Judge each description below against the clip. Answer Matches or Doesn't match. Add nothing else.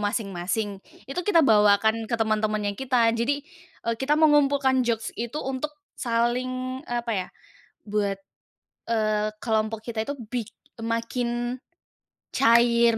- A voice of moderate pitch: Doesn't match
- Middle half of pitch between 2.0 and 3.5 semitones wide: Matches